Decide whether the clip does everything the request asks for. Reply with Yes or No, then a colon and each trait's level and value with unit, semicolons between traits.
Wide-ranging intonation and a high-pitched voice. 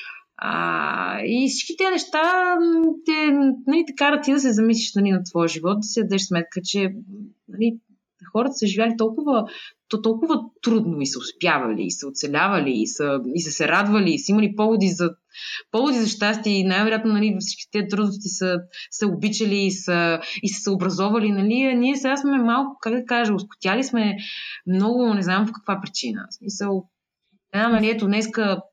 No: average, 3.7 semitones; high, 215 Hz